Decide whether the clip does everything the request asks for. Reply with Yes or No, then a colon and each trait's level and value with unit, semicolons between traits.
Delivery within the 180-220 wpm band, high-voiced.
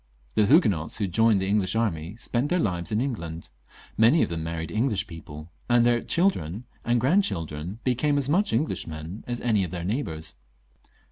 No: average, 185 wpm; low, 105 Hz